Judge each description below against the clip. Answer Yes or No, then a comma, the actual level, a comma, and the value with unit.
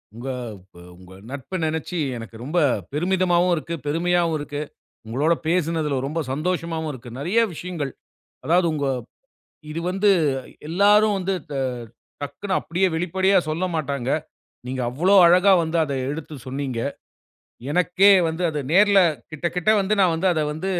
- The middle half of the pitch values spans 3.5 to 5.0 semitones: Yes, average, 3.8 semitones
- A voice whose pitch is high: No, medium, 165 Hz